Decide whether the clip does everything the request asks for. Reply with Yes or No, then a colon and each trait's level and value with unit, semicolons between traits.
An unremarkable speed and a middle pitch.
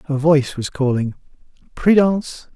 No: slow, 115 wpm; medium, 145 Hz